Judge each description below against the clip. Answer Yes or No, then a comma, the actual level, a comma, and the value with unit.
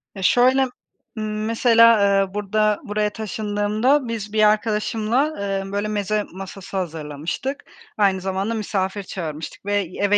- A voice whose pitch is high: Yes, high, 210 Hz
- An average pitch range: No, narrow, 2.0 semitones